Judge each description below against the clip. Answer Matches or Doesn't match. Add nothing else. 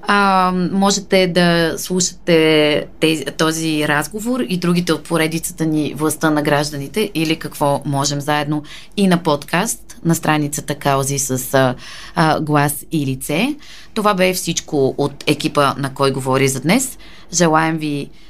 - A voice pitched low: Doesn't match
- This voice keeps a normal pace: Matches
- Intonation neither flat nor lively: Matches